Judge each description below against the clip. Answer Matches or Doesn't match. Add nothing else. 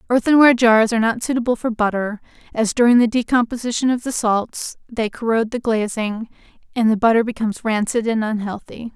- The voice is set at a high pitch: Matches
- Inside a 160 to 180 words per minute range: Matches